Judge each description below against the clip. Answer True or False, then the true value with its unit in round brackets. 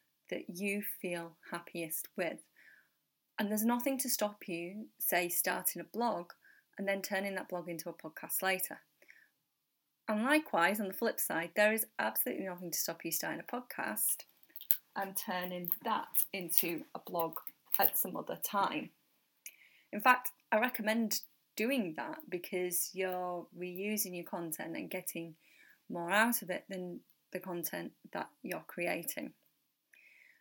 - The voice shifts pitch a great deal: False (3.7 semitones)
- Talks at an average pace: True (145 wpm)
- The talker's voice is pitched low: False (190 Hz)